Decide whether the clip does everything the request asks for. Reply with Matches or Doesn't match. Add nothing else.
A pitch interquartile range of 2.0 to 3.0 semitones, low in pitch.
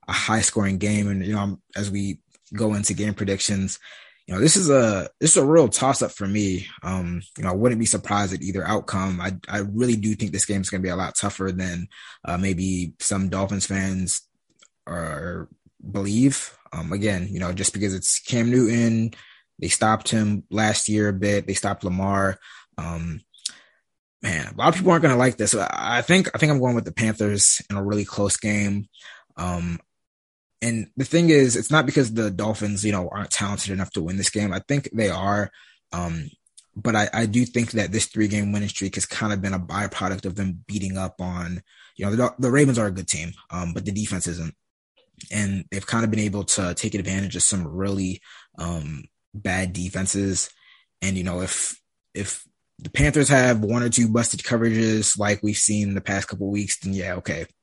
Matches